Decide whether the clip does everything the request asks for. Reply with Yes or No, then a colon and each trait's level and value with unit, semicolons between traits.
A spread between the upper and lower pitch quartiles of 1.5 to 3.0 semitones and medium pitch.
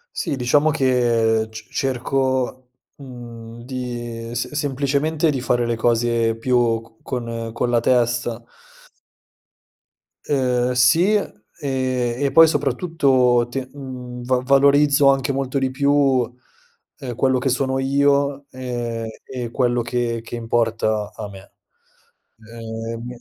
No: narrow, 2.5 semitones; low, 125 Hz